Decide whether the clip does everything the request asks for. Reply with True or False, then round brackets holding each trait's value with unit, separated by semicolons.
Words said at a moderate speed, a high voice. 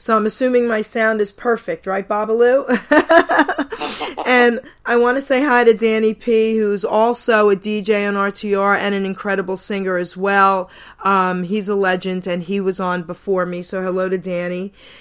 True (175 wpm; 205 Hz)